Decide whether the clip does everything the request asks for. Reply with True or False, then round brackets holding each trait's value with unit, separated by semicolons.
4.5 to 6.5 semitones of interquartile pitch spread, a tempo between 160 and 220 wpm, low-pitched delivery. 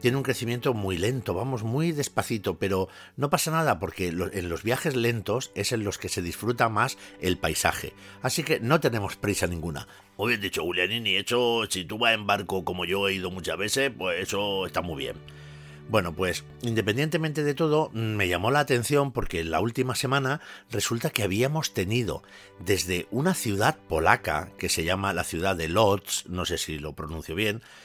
True (5.2 semitones; 190 wpm; 105 Hz)